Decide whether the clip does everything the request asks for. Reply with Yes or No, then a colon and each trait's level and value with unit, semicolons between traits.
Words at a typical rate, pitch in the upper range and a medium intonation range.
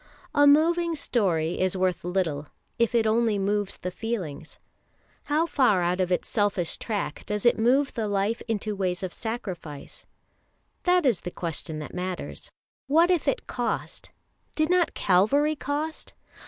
No: average, 155 wpm; high, 210 Hz; wide, 7.7 semitones